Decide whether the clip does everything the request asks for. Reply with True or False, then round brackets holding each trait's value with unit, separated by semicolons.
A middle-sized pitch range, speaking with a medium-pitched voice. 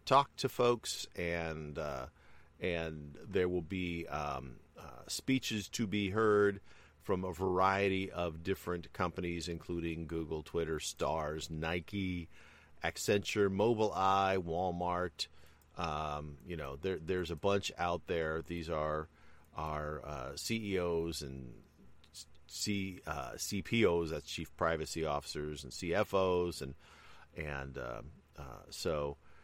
False (4.1 semitones; 85 Hz)